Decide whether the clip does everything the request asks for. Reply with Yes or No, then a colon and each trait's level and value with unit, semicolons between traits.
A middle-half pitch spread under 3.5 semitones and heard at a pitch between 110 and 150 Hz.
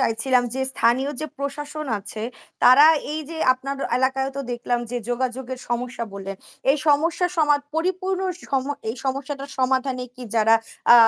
No: average, 2.8 semitones; very high, 265 Hz